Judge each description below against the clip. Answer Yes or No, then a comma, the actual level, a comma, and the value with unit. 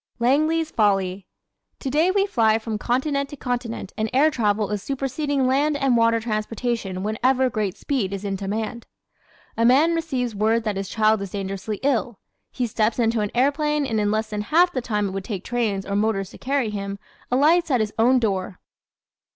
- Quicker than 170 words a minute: Yes, average, 190 wpm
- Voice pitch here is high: Yes, high, 230 Hz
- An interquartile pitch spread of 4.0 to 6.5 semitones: Yes, average, 4.5 semitones